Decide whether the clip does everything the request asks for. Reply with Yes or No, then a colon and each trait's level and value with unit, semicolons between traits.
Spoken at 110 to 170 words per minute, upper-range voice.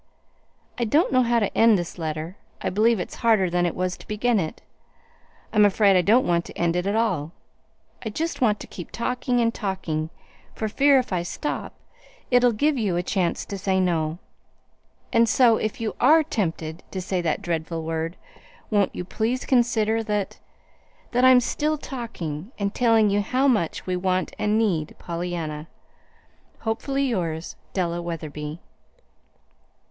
Yes: average, 165 wpm; high, 200 Hz